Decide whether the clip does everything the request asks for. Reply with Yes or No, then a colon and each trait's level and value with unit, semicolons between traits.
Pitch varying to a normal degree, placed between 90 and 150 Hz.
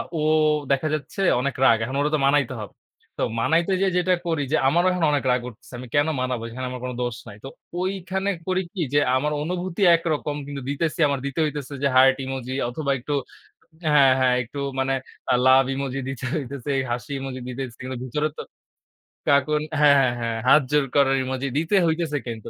Yes: average, 3.1 semitones; medium, 140 Hz